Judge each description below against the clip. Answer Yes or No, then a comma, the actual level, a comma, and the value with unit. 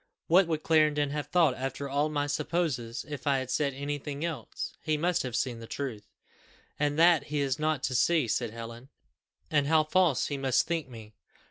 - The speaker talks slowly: No, average, 200 wpm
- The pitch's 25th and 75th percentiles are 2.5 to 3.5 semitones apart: Yes, average, 3.2 semitones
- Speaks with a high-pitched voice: No, medium, 145 Hz